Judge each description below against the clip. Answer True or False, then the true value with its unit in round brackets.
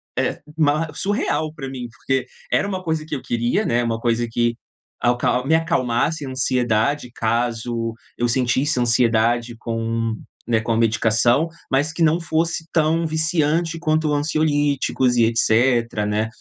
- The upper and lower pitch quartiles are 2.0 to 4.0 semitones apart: False (5.0 semitones)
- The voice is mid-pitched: False (125 Hz)